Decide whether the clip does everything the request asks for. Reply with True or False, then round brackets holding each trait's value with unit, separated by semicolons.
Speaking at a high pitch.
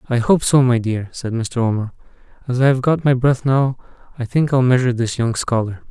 False (125 Hz)